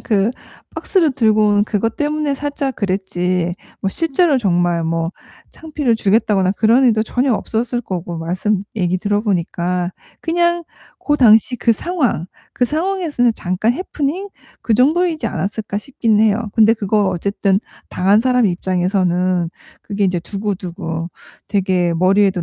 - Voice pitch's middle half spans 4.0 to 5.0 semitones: No, wide, 5.4 semitones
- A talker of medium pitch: No, high, 210 Hz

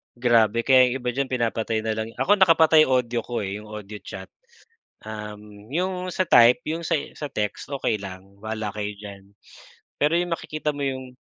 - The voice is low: Yes, low, 120 Hz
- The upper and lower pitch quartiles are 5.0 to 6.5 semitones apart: Yes, wide, 5.6 semitones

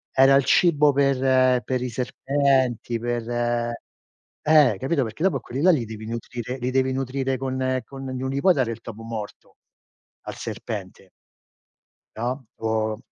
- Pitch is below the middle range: Yes, low, 130 Hz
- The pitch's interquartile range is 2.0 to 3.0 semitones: Yes, narrow, 2.4 semitones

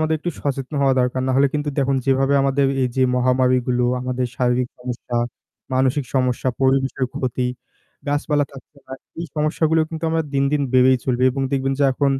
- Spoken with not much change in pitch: Yes, narrow, 1.9 semitones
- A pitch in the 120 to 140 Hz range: Yes, low, 135 Hz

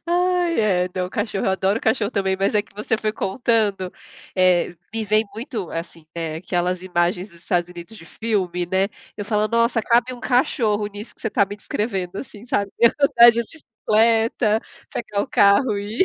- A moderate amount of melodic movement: Yes, average, 3.5 semitones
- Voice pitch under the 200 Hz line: No, high, 210 Hz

